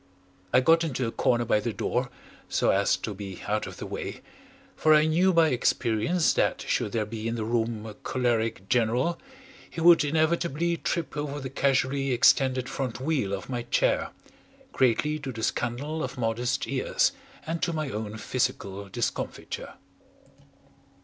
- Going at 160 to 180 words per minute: Yes, average, 165 wpm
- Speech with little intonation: No, average, 5.2 semitones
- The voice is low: Yes, low, 125 Hz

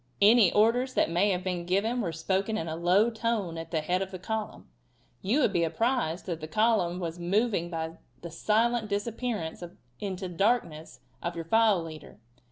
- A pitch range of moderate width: Yes, average, 4.7 semitones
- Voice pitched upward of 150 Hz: Yes, high, 190 Hz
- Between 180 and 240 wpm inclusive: Yes, average, 185 wpm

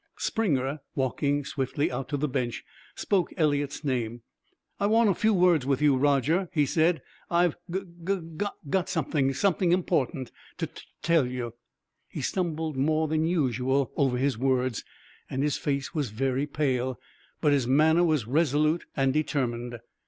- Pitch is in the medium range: Yes, medium, 145 Hz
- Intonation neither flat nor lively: Yes, average, 4.1 semitones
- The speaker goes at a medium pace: Yes, average, 155 wpm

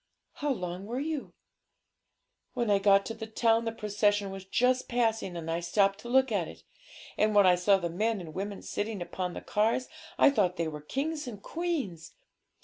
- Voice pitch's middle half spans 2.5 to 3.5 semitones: No, average, 4.5 semitones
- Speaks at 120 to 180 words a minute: No, average, 195 wpm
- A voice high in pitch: Yes, high, 205 Hz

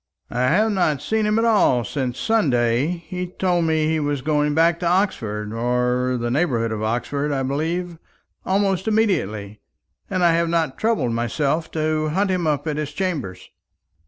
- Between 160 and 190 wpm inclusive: Yes, average, 170 wpm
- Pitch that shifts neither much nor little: No, wide, 6.4 semitones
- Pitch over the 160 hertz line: No, medium, 155 Hz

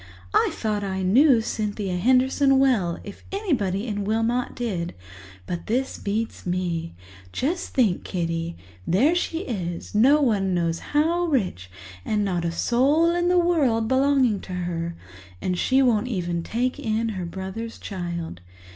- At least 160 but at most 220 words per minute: No, average, 145 wpm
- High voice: Yes, high, 215 Hz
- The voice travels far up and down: Yes, wide, 6.6 semitones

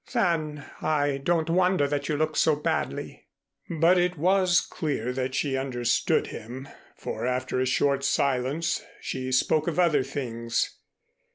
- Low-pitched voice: No, medium, 145 Hz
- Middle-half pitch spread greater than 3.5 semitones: Yes, average, 4.1 semitones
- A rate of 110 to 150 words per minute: Yes, average, 145 wpm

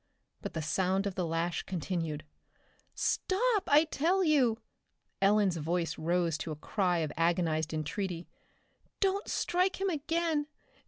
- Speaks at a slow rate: Yes, slow, 130 wpm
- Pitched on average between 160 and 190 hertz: Yes, medium, 185 Hz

